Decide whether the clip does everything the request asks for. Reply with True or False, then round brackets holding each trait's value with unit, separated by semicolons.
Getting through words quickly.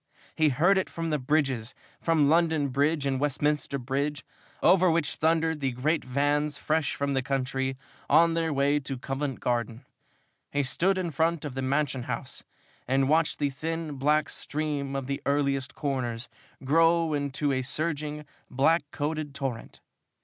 False (155 wpm)